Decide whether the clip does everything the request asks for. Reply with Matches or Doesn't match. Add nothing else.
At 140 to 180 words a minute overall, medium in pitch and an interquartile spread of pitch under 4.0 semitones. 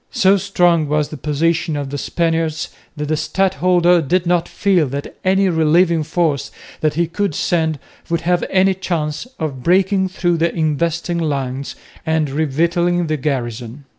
Matches